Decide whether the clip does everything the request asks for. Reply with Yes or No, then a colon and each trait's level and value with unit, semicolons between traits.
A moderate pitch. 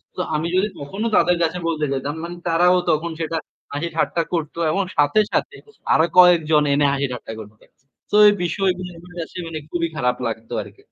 Yes: medium, 165 Hz